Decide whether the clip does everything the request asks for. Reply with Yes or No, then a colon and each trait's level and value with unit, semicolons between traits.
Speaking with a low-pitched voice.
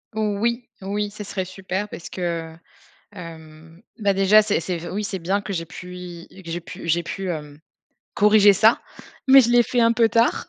No: high, 195 Hz